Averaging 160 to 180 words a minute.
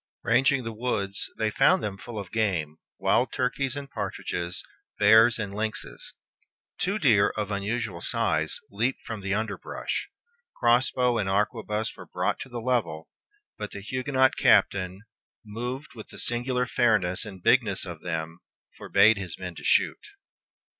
No: average, 150 wpm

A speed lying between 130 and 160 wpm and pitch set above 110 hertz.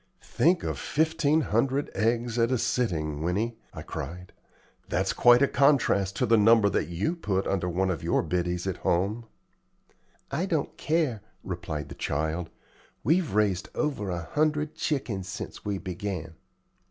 No: average, 155 wpm; low, 105 Hz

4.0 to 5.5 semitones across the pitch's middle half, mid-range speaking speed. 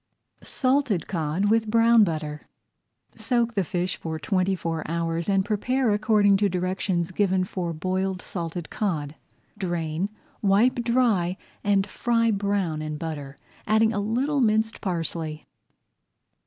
No: average, 4.5 semitones; slow, 130 wpm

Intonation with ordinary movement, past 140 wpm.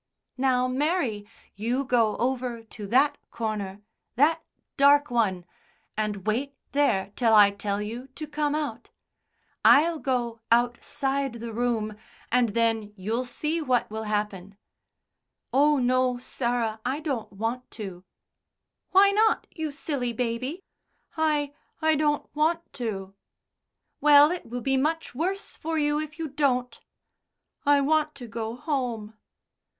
No: average, 4.8 semitones; slow, 135 wpm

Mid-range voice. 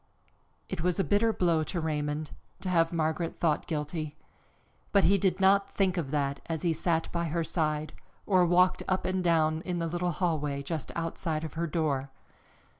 Yes: medium, 165 Hz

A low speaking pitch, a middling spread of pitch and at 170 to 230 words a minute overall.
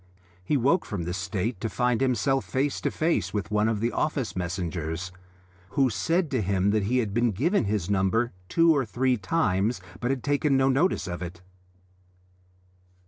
No: low, 115 Hz; wide, 5.8 semitones; average, 180 wpm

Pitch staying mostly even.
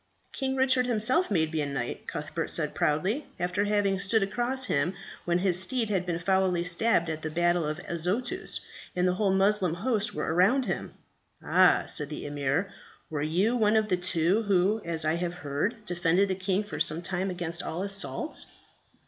No: average, 3.8 semitones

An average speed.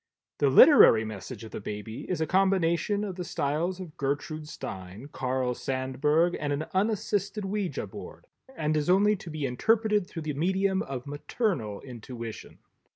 Yes: average, 160 wpm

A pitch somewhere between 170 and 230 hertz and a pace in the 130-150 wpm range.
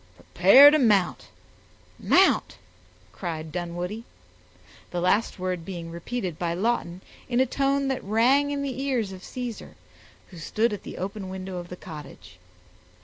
Yes: high, 190 Hz; average, 145 wpm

